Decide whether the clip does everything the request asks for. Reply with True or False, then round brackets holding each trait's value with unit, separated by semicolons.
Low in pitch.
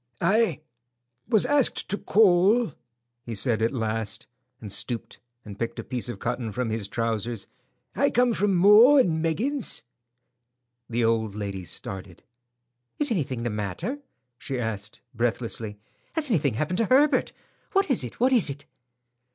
True (125 Hz)